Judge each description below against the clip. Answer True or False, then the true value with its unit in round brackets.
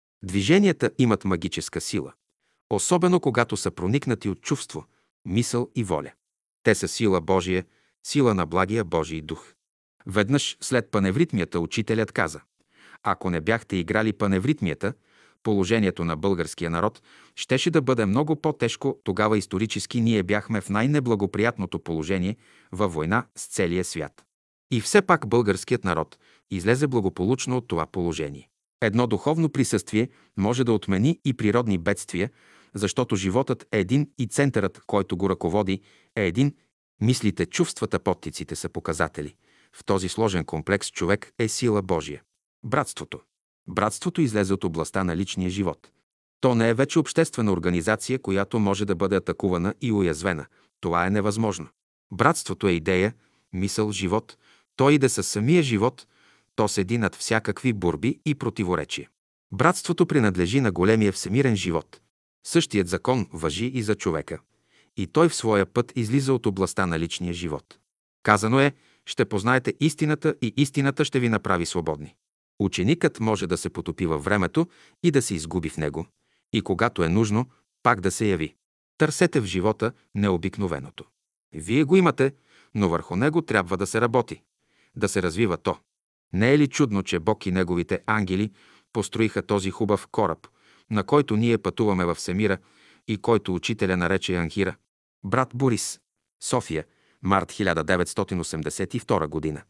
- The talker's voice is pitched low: True (105 Hz)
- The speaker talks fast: False (145 wpm)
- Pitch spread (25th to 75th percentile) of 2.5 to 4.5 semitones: False (4.9 semitones)